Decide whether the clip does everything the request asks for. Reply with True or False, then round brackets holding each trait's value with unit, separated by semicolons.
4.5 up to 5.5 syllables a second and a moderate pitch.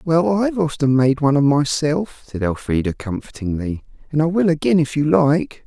True (5.2 syllables/s; 145 Hz)